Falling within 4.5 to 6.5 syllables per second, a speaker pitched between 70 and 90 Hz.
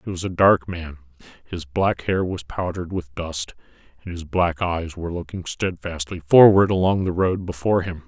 Yes: 5.0 syllables/s; very low, 85 Hz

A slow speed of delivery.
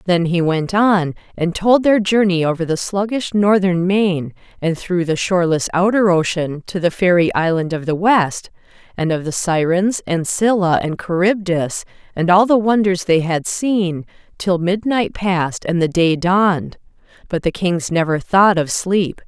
No: average, 170 wpm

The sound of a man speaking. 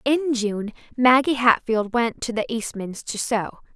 No: female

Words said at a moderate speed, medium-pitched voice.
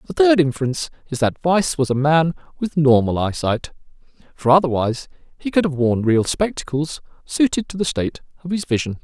Yes: average, 180 wpm; medium, 150 Hz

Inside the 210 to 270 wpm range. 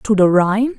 Yes: fast, 230 wpm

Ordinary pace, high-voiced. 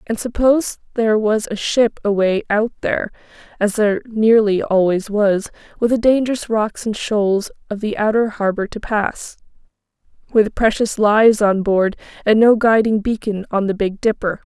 Yes: average, 160 wpm; high, 215 Hz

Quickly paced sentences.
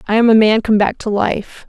Yes: fast, 285 wpm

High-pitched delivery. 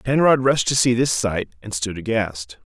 No: low, 115 Hz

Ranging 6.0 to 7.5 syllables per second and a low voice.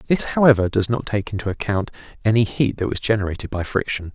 Yes: 6.4 syllables/s; low, 110 Hz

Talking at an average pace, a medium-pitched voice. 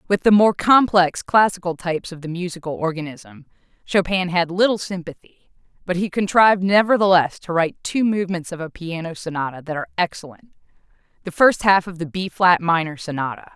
Yes: average, 165 wpm; medium, 175 Hz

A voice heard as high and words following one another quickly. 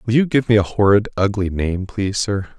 No: low, 105 Hz; fast, 230 wpm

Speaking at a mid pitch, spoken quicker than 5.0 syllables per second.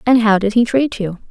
No: high, 220 Hz; 5.5 syllables/s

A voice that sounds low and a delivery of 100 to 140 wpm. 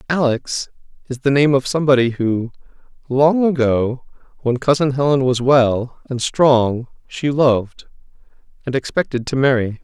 Yes: low, 130 Hz; slow, 135 wpm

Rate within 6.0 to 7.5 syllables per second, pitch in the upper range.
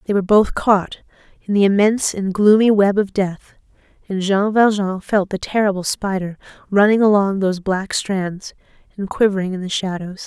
No: 5.1 syllables/s; high, 195 Hz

